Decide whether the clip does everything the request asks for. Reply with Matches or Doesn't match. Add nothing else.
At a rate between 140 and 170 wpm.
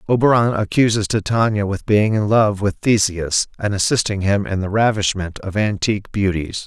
Matches